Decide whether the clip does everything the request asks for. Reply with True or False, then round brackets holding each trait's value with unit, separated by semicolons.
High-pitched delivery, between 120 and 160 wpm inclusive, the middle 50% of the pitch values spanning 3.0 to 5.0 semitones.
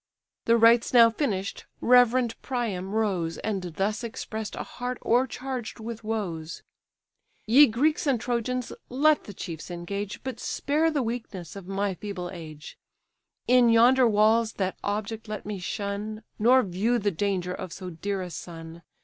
True (215 Hz; 150 wpm; 4.2 semitones)